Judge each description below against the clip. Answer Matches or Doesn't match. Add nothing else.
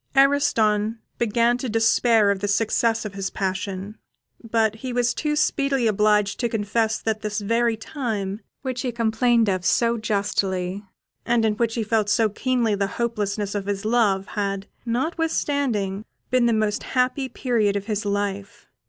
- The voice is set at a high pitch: Matches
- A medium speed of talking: Matches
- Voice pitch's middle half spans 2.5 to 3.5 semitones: Matches